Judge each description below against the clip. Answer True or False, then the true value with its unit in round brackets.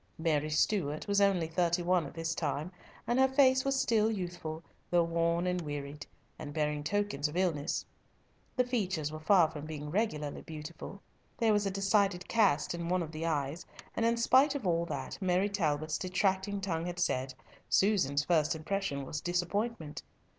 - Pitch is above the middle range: False (175 Hz)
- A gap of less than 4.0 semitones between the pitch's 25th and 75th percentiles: False (4.6 semitones)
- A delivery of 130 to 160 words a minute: False (175 wpm)